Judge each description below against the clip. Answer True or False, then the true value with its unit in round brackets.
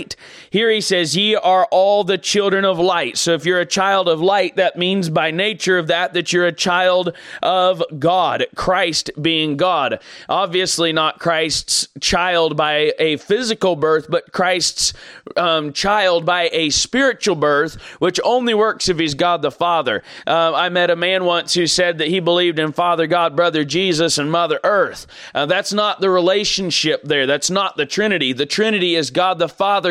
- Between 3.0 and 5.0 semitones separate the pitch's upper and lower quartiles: False (2.6 semitones)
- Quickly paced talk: False (185 wpm)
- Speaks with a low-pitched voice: False (175 Hz)